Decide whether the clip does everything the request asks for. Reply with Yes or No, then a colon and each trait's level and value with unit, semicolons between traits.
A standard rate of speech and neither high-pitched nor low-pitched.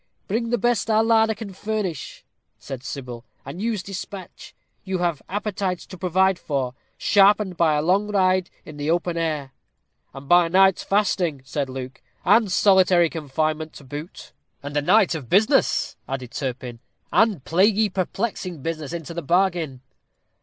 Yes: average, 155 wpm; medium, 175 Hz